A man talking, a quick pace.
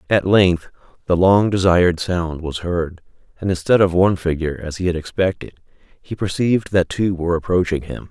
No: male; average, 180 wpm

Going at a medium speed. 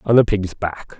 No: fast, 240 wpm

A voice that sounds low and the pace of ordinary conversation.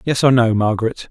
No: low, 120 Hz; fast, 215 wpm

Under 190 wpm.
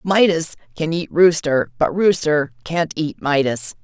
Yes: average, 140 wpm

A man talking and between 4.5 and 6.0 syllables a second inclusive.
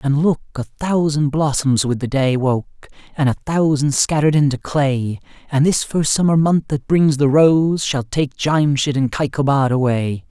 No: male; 4.3 syllables/s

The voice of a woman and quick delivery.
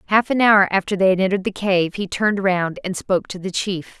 Yes: female; fast, 255 wpm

